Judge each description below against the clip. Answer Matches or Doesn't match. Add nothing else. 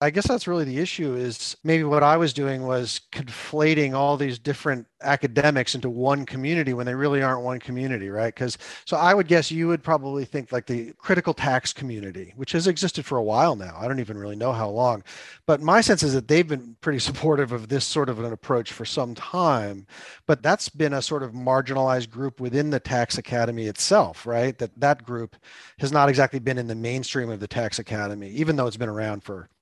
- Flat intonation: Doesn't match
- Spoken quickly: Matches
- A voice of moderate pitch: Doesn't match